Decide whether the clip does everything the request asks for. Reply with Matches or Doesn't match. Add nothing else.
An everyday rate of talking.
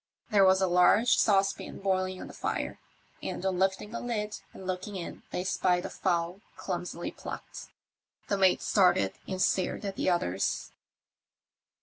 Matches